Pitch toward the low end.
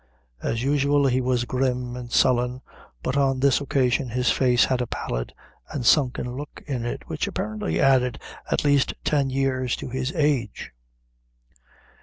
Yes: low, 130 Hz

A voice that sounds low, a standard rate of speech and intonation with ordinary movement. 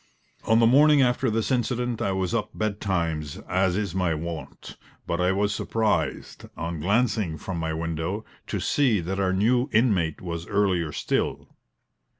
Yes: very low, 95 Hz; average, 155 wpm; average, 5.0 semitones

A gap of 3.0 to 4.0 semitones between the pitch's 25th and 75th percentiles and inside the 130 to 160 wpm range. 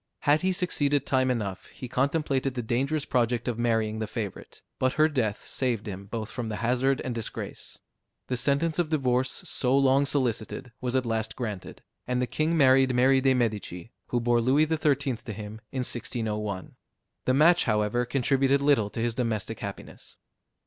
No: average, 3.4 semitones; average, 175 wpm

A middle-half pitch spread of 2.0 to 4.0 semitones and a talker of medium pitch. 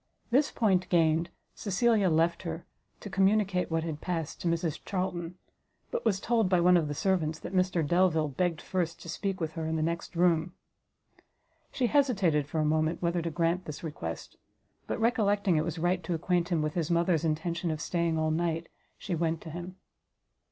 Yes: narrow, 2.4 semitones; medium, 170 Hz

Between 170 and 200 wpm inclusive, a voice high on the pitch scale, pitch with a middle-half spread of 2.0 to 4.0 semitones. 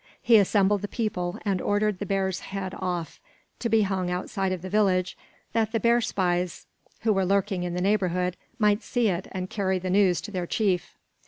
Yes: average, 195 wpm; high, 195 Hz; narrow, 2.4 semitones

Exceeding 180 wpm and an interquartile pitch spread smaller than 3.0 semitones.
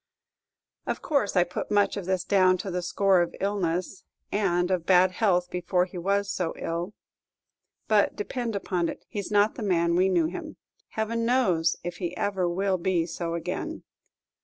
No: average, 175 wpm; narrow, 2.5 semitones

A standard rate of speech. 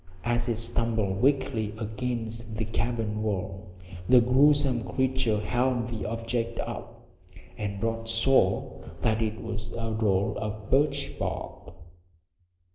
No: slow, 120 wpm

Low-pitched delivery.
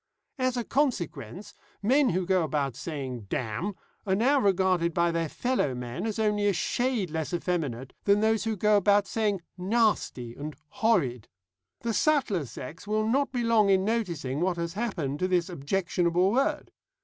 No: high, 190 Hz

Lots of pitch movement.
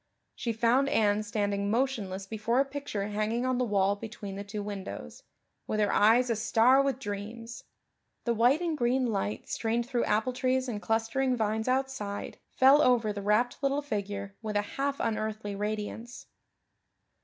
No: average, 3.5 semitones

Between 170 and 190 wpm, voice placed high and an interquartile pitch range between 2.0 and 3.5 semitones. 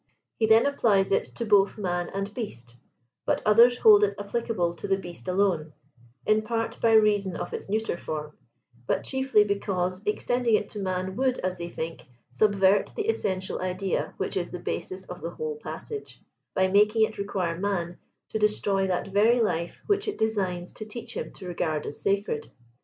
Yes: average, 180 wpm; high, 200 Hz; average, 3.2 semitones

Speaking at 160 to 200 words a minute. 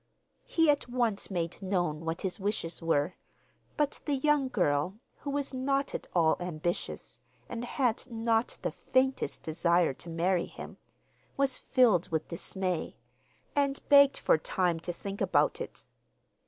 No: average, 145 wpm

